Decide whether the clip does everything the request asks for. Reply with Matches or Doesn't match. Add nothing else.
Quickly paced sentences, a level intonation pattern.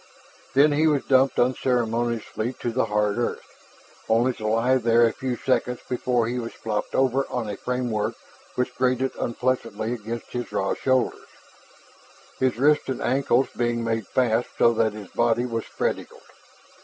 Doesn't match